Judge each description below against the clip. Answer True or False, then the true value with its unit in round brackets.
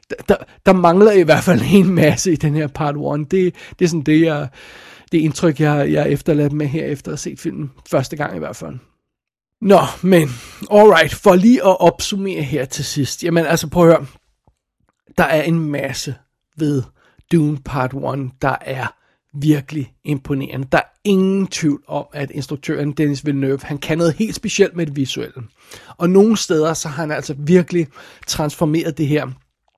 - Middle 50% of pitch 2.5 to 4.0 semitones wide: True (2.9 semitones)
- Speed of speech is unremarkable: True (185 wpm)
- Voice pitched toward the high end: False (155 Hz)